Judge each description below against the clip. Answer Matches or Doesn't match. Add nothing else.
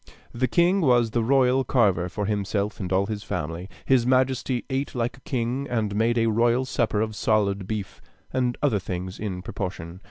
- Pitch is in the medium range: Doesn't match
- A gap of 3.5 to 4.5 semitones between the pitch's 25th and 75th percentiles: Matches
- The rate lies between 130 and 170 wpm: Doesn't match